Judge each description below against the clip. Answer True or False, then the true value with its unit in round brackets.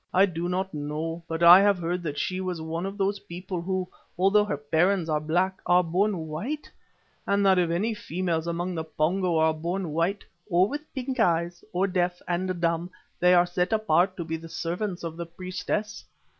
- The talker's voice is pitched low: False (180 Hz)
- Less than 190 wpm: False (200 wpm)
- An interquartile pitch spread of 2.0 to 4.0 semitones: True (2.4 semitones)